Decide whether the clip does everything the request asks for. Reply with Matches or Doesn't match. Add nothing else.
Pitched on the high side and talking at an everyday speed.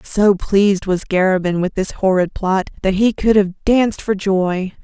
Matches